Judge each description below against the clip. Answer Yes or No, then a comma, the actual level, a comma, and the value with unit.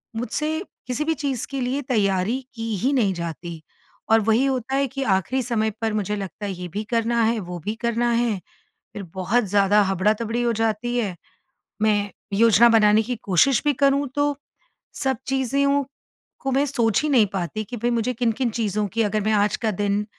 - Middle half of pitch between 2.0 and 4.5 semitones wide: Yes, average, 3.3 semitones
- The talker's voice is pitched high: Yes, high, 225 Hz